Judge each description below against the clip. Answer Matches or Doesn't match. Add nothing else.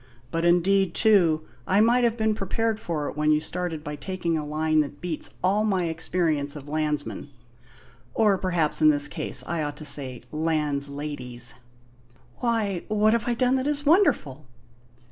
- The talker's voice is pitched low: Doesn't match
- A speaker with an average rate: Matches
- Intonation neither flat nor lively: Doesn't match